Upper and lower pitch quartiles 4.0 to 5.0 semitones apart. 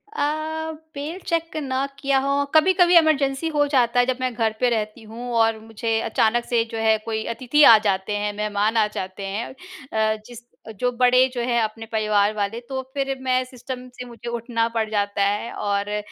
No: average, 3.6 semitones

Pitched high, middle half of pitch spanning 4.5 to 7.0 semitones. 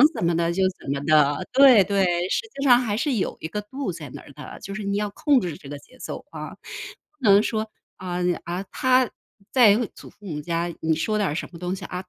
Yes: high, 195 Hz; average, 4.8 semitones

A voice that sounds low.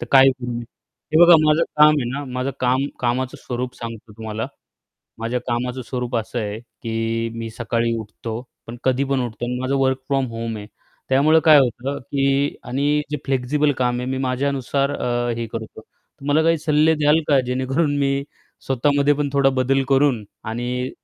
Yes: low, 130 Hz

